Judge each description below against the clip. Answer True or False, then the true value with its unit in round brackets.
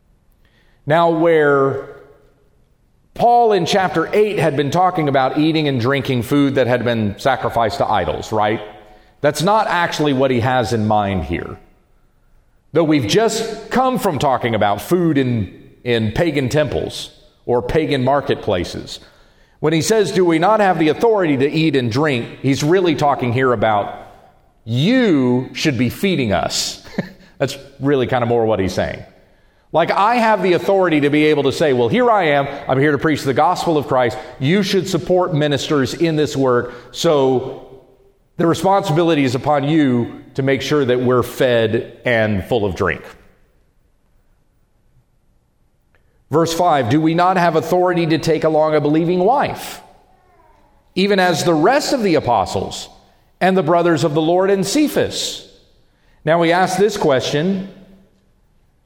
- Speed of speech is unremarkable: True (155 wpm)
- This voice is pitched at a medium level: True (150 Hz)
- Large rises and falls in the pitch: True (5.7 semitones)